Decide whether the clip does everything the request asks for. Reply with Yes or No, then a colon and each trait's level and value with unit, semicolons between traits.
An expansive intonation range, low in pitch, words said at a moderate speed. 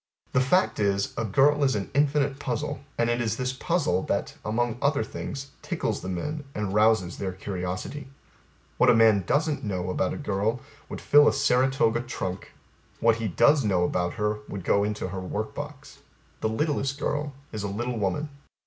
Yes: wide, 5.7 semitones; low, 115 Hz; average, 185 wpm